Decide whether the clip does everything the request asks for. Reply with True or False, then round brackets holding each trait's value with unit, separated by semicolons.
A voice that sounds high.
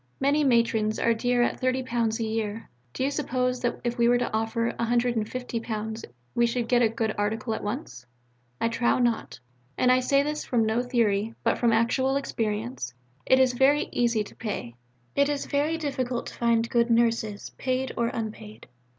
True (235 Hz)